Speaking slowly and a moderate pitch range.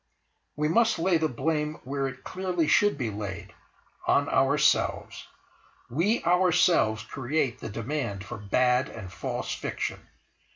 No: slow, 130 wpm; wide, 6.7 semitones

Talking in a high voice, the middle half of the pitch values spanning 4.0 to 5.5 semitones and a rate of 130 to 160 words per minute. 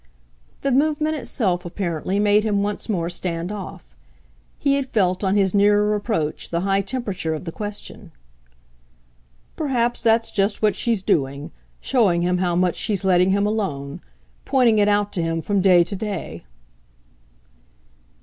No: high, 200 Hz; average, 3.4 semitones; average, 150 wpm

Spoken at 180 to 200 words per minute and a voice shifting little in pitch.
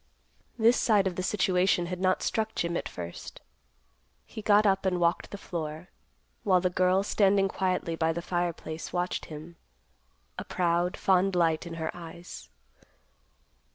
No: average, 155 wpm; narrow, 2.2 semitones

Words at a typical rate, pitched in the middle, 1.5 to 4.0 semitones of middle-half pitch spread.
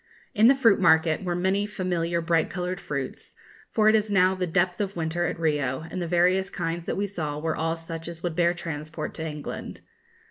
No: fast, 210 wpm; medium, 175 Hz; average, 2.7 semitones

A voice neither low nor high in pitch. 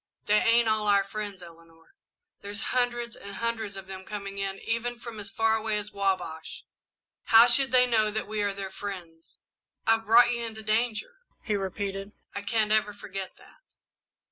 No: high, 210 Hz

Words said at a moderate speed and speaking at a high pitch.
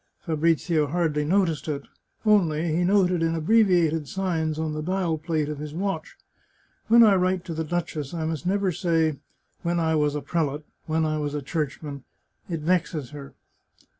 No: average, 190 wpm; medium, 160 Hz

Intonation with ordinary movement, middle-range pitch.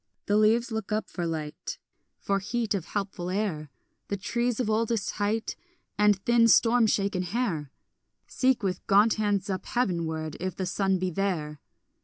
No: average, 3.4 semitones; high, 200 Hz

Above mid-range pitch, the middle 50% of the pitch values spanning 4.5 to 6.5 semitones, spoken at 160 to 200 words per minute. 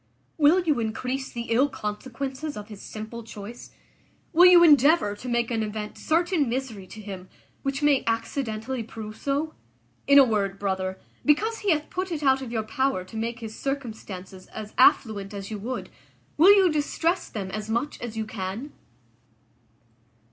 Yes: high, 235 Hz; average, 5.1 semitones; average, 170 wpm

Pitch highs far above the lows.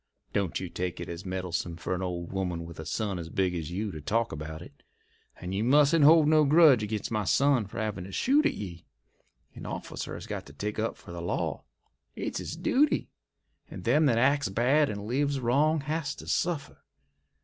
Yes: wide, 8.2 semitones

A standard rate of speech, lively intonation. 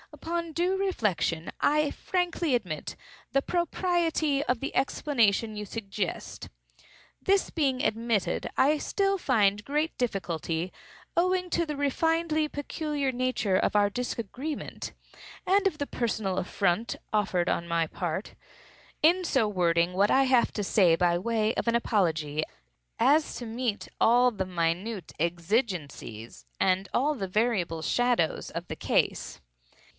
No: slow, 130 wpm; wide, 8.0 semitones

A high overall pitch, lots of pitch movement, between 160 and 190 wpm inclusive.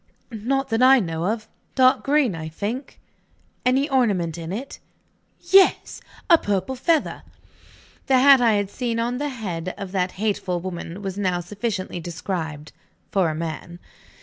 No: high, 205 Hz; wide, 6.3 semitones; average, 150 wpm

